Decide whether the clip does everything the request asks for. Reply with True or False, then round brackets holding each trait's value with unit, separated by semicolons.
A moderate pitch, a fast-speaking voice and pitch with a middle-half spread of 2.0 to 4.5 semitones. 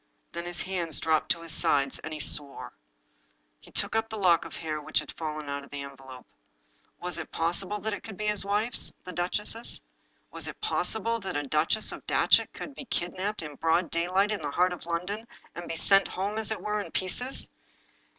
False (175 Hz; 210 wpm; 5.0 semitones)